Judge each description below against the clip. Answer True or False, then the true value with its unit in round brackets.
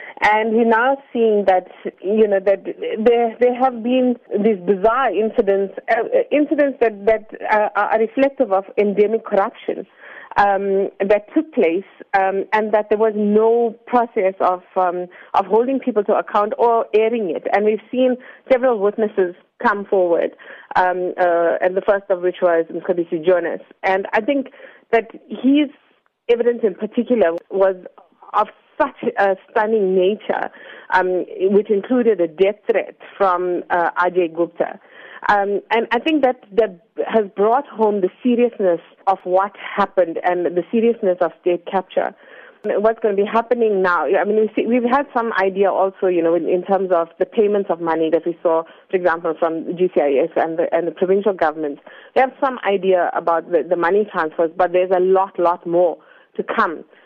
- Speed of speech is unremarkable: True (170 wpm)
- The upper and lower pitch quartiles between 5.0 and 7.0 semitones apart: False (4.0 semitones)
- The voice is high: True (200 Hz)